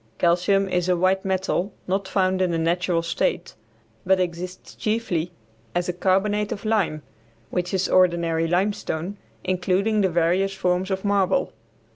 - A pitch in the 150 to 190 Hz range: Yes, medium, 185 Hz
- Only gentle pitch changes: Yes, narrow, 1.9 semitones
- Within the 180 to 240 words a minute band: No, average, 145 wpm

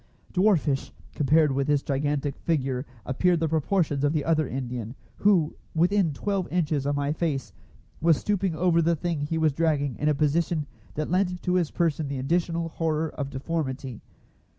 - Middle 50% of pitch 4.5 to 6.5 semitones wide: No, average, 3.1 semitones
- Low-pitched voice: No, medium, 155 Hz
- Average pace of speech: Yes, average, 170 wpm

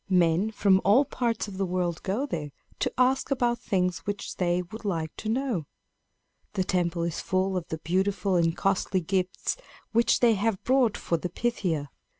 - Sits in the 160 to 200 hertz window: Yes, high, 190 Hz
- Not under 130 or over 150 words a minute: No, average, 175 wpm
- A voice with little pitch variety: No, average, 4.1 semitones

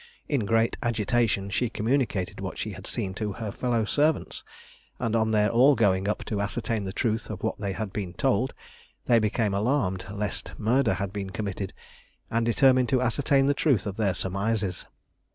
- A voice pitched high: No, low, 110 Hz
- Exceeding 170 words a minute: Yes, average, 180 wpm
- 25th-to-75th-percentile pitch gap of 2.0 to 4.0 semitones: Yes, average, 3.3 semitones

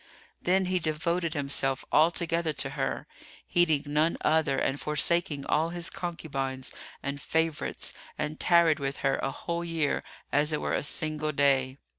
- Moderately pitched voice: Yes, medium, 155 Hz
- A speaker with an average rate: Yes, average, 155 wpm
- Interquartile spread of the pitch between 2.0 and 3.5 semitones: Yes, average, 3.1 semitones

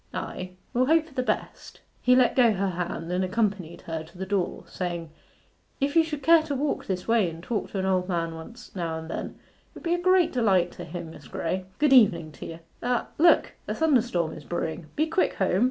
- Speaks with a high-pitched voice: Yes, high, 195 Hz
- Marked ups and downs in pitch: Yes, wide, 7.2 semitones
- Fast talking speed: Yes, fast, 225 wpm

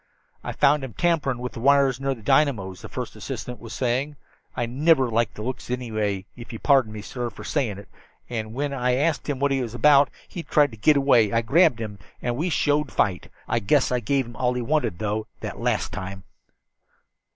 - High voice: No, low, 125 Hz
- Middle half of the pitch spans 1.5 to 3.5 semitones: No, average, 4.1 semitones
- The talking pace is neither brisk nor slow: No, fast, 220 wpm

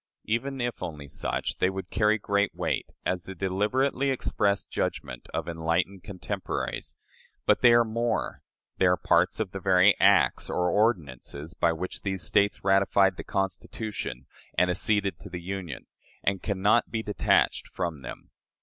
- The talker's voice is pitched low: Yes, very low, 95 Hz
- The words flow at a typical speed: Yes, average, 160 wpm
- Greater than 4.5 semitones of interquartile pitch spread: No, average, 3.1 semitones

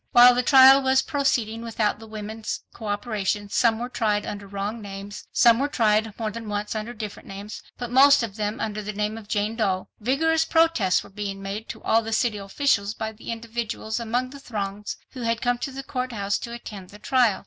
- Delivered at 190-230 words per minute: Yes, average, 200 wpm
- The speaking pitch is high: Yes, high, 220 Hz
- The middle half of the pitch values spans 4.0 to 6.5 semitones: No, average, 2.8 semitones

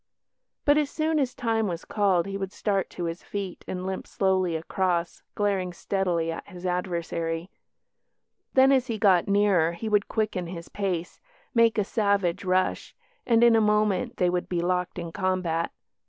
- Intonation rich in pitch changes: No, average, 3.2 semitones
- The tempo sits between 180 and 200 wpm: No, average, 170 wpm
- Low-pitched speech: No, high, 190 Hz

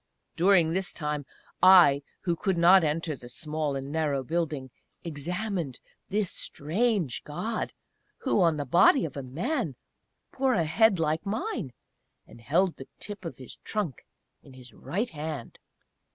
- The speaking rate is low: No, average, 150 wpm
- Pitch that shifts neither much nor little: Yes, average, 5.0 semitones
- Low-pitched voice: No, medium, 165 Hz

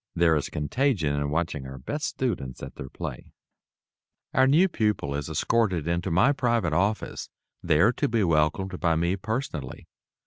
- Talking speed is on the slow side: No, average, 165 wpm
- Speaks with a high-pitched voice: No, very low, 85 Hz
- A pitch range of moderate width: No, wide, 7.2 semitones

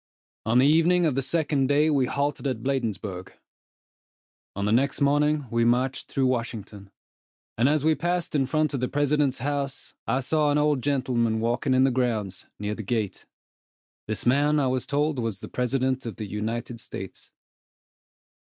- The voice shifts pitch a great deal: No, average, 3.8 semitones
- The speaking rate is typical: Yes, average, 170 wpm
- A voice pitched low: Yes, low, 130 Hz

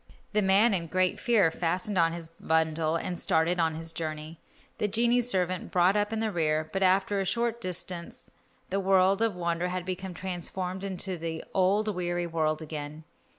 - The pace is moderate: Yes, average, 175 wpm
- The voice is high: No, medium, 180 Hz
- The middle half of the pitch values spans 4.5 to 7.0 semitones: No, average, 2.9 semitones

